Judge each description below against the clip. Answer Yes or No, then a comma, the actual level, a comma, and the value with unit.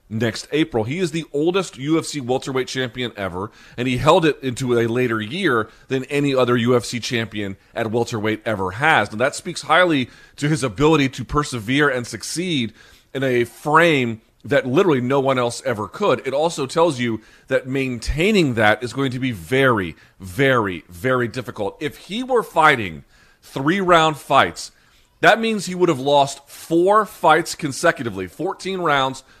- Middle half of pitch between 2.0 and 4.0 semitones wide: No, average, 4.5 semitones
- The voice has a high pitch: No, low, 130 Hz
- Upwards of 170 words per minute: No, average, 165 wpm